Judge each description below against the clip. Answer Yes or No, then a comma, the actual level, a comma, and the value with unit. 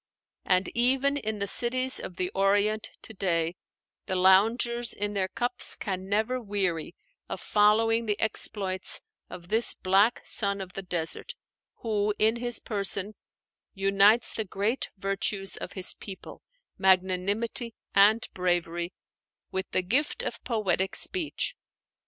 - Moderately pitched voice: No, high, 200 Hz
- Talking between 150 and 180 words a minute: No, slow, 135 wpm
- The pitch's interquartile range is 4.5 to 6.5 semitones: No, average, 3.2 semitones